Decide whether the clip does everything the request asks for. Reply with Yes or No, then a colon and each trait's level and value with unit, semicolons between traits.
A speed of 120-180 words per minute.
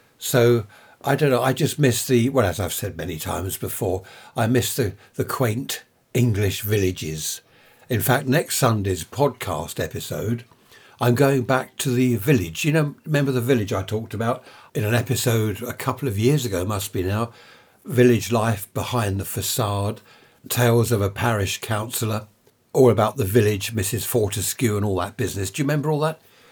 Yes: average, 175 wpm